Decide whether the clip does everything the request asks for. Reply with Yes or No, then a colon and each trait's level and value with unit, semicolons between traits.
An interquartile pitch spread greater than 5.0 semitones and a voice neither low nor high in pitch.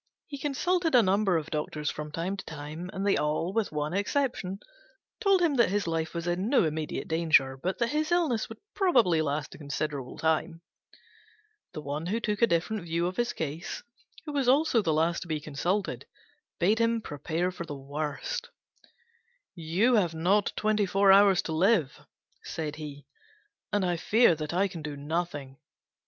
Yes: wide, 5.6 semitones; medium, 175 Hz